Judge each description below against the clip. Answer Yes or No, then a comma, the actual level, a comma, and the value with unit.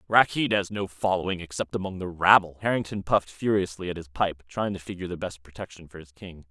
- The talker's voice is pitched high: No, very low, 90 Hz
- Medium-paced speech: No, fast, 210 wpm